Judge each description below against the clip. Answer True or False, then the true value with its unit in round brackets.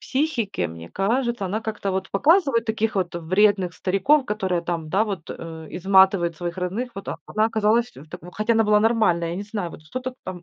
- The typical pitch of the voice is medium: False (195 Hz)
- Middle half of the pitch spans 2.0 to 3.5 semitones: False (4.2 semitones)